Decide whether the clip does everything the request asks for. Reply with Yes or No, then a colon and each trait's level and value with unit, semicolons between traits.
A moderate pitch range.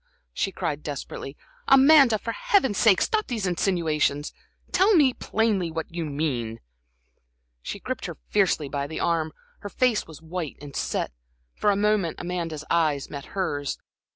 No: wide, 6.3 semitones